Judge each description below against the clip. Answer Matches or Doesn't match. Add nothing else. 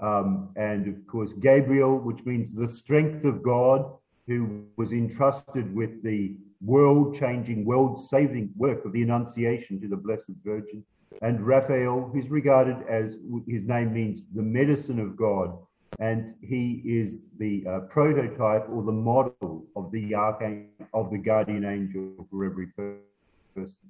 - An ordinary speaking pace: Matches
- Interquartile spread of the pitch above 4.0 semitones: Doesn't match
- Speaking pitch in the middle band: Doesn't match